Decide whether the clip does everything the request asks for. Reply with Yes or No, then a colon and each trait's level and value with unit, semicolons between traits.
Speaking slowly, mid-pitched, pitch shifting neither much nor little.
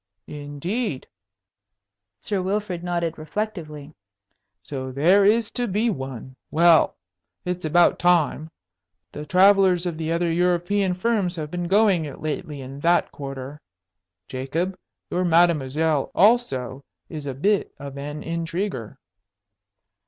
Yes: slow, 120 wpm; medium, 170 Hz; average, 4.3 semitones